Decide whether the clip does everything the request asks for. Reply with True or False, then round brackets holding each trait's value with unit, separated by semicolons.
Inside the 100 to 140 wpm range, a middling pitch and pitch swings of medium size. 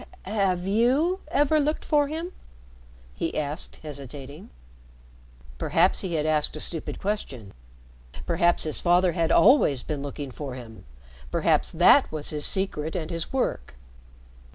False (135 wpm; 165 Hz; 5.9 semitones)